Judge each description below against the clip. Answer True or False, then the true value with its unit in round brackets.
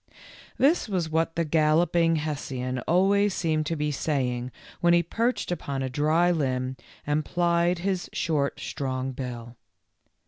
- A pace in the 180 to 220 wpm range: False (140 wpm)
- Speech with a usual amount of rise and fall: True (4.4 semitones)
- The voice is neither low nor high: True (155 Hz)